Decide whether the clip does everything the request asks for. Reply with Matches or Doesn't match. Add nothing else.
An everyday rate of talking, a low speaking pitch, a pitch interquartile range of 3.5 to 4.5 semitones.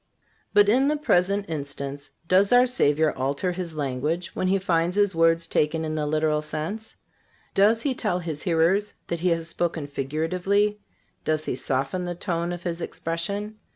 Doesn't match